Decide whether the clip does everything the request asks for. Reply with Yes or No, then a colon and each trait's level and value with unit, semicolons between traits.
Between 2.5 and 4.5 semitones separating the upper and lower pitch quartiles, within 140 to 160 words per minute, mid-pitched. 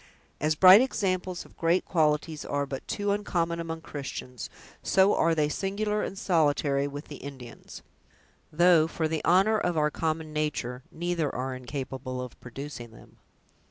Yes: average, 3.9 semitones; average, 155 wpm; medium, 155 Hz